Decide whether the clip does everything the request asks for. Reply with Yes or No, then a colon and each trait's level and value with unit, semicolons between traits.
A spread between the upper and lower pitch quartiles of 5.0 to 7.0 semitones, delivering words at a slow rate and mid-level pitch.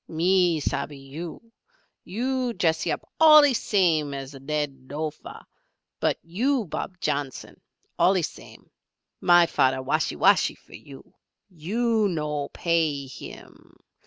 Yes: average, 5.3 semitones; slow, 115 wpm; medium, 165 Hz